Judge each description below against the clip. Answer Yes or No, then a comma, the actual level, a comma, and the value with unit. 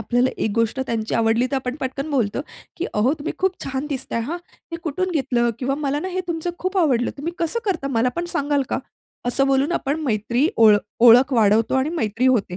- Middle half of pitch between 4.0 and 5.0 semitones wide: Yes, average, 4.4 semitones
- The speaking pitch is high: Yes, very high, 265 Hz